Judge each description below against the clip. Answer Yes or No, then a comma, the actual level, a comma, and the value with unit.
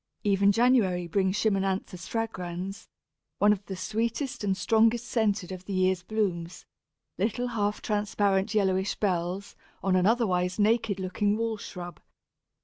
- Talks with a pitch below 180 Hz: No, high, 200 Hz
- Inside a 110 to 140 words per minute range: Yes, slow, 135 wpm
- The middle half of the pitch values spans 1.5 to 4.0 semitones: Yes, average, 2.9 semitones